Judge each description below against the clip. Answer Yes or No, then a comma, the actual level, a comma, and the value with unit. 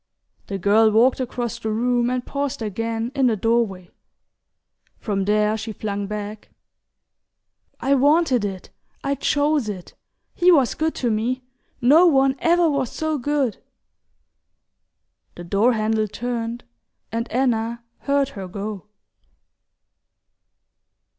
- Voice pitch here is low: No, high, 235 Hz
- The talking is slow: Yes, slow, 120 wpm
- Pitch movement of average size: Yes, average, 4.2 semitones